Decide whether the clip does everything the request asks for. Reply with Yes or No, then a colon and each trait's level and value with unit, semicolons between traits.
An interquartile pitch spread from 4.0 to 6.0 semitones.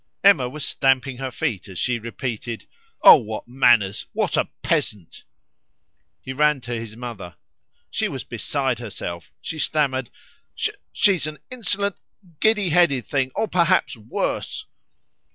Yes: average, 4.8 semitones